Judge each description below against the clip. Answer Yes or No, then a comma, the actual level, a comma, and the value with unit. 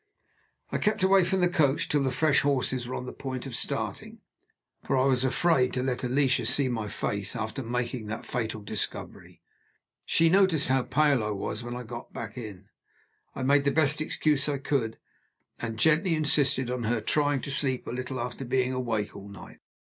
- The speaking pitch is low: Yes, low, 130 Hz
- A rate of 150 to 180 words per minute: No, average, 190 wpm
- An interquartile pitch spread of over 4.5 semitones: No, average, 3.2 semitones